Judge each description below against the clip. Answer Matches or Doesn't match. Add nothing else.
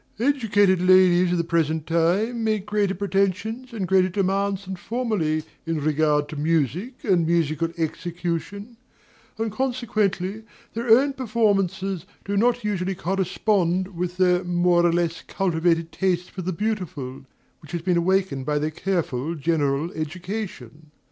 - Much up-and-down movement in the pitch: Doesn't match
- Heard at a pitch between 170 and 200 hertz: Matches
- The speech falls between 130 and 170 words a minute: Matches